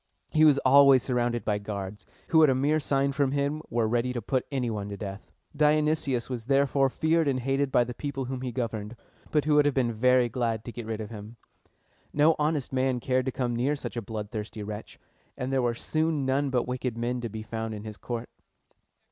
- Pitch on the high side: No, low, 125 Hz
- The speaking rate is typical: No, fast, 220 wpm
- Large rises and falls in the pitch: No, average, 3.4 semitones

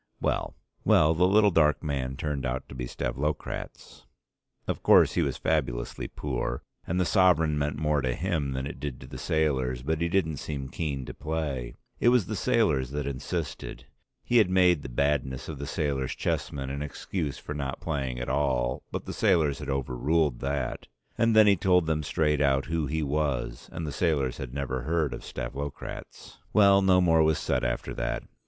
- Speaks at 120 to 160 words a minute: No, average, 190 wpm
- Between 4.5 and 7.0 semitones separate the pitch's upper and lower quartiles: No, average, 3.6 semitones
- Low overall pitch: Yes, very low, 75 Hz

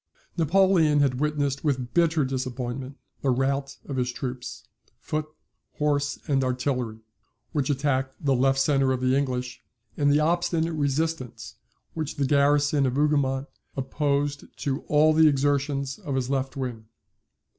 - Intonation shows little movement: Yes, narrow, 2.1 semitones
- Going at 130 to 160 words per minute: Yes, average, 145 wpm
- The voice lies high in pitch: No, medium, 140 Hz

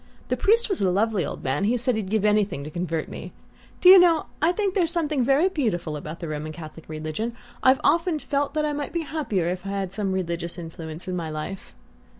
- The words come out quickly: Yes, fast, 225 wpm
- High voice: Yes, high, 205 Hz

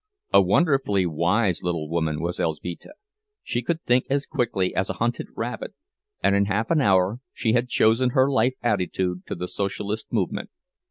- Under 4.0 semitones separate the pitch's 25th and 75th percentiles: No, wide, 5.4 semitones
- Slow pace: No, average, 170 wpm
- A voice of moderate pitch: No, low, 105 Hz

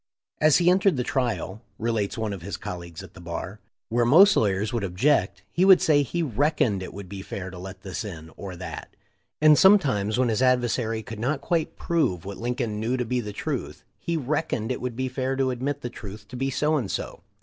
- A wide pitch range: Yes, wide, 5.9 semitones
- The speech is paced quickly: Yes, fast, 230 wpm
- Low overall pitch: Yes, low, 120 Hz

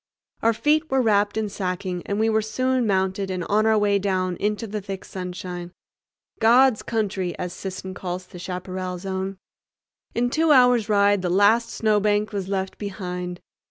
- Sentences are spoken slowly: No, average, 160 wpm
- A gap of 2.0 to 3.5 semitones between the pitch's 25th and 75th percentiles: Yes, average, 2.9 semitones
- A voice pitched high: Yes, high, 200 Hz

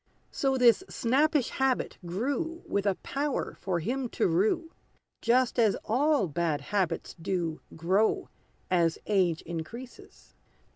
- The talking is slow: Yes, slow, 125 wpm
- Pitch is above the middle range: Yes, high, 215 Hz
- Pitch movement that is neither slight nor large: No, wide, 7.5 semitones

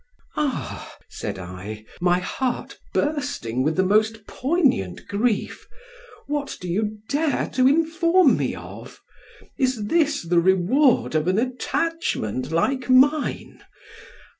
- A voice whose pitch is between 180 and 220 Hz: No, high, 240 Hz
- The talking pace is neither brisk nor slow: No, slow, 115 wpm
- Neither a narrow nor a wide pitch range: No, wide, 8.5 semitones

